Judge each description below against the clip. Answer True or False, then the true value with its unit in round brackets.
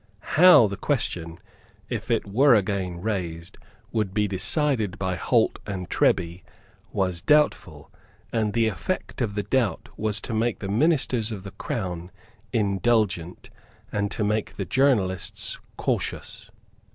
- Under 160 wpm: True (135 wpm)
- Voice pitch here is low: True (105 Hz)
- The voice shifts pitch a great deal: False (3.7 semitones)